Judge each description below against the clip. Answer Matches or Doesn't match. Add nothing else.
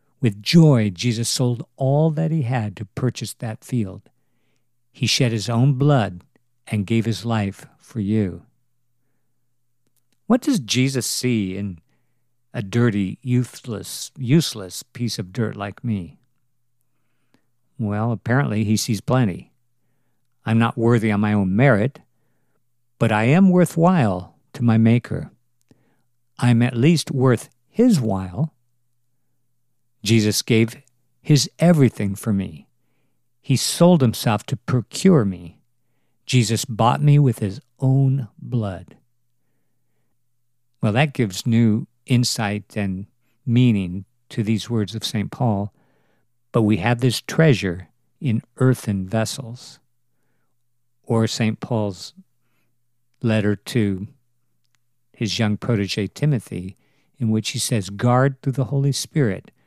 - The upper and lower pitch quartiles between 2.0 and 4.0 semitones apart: Matches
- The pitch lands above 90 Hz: Matches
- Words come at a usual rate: Doesn't match